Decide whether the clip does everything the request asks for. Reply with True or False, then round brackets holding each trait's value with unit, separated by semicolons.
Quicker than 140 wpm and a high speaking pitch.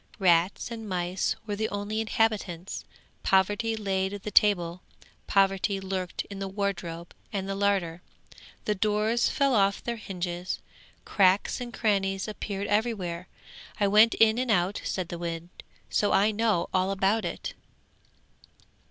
False (135 wpm; 200 Hz)